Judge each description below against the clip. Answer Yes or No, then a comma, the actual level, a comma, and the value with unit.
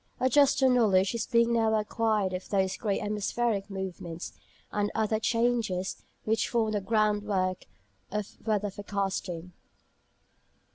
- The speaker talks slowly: Yes, slow, 125 wpm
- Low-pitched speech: No, high, 210 Hz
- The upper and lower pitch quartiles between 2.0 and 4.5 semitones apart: Yes, average, 2.9 semitones